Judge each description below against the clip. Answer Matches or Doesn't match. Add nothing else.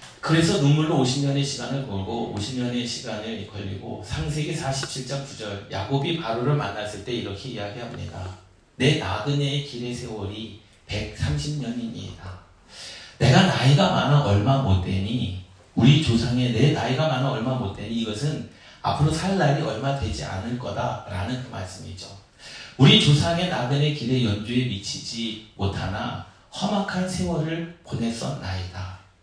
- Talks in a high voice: Doesn't match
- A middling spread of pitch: Doesn't match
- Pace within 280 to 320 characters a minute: Matches